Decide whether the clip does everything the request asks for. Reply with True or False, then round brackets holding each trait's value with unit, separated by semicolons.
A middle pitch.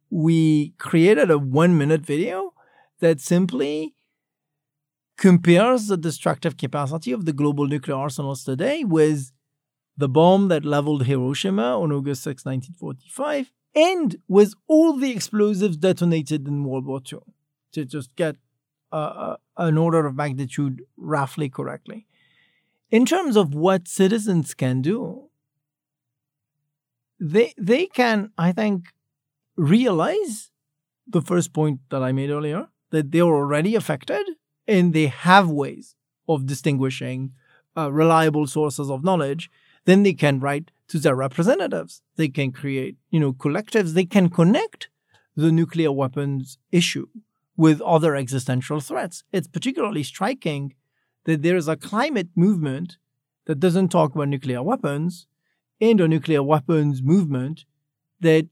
True (155 Hz)